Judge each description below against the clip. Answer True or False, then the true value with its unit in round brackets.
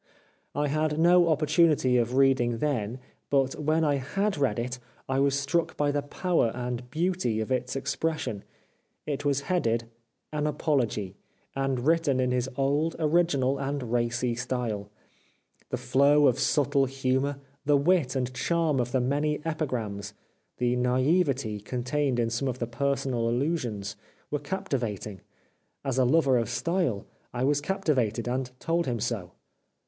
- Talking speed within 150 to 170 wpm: True (155 wpm)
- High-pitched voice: False (135 Hz)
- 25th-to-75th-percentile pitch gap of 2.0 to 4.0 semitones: True (3.4 semitones)